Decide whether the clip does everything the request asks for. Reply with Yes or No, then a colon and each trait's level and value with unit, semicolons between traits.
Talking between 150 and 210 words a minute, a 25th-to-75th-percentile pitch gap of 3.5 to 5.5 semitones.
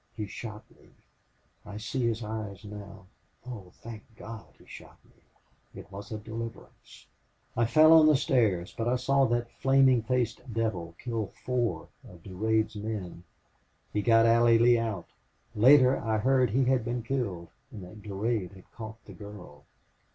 No: average, 165 wpm; average, 2.9 semitones